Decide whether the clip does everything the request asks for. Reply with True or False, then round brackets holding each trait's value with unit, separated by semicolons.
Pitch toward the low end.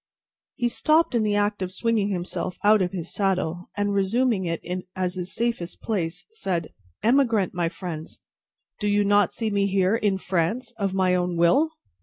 False (195 Hz)